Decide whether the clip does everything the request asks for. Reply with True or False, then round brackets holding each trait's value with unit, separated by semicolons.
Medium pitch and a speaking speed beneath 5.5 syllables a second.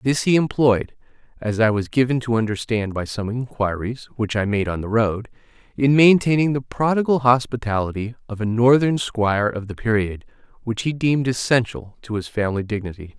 False (115 Hz; 4.0 syllables/s)